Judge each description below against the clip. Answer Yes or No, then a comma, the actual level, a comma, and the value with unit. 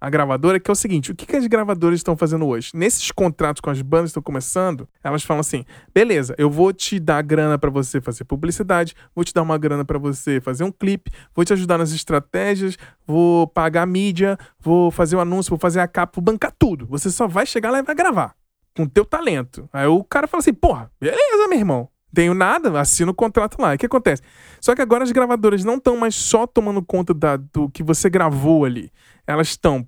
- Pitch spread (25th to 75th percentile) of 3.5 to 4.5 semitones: No, average, 5.2 semitones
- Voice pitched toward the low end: No, medium, 170 Hz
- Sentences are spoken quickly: Yes, fast, 230 wpm